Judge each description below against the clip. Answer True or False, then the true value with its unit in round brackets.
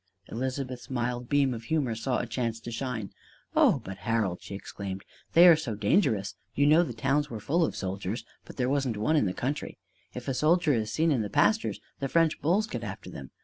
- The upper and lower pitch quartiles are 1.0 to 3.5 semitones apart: False (5.0 semitones)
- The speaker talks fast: True (215 wpm)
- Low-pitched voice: True (125 Hz)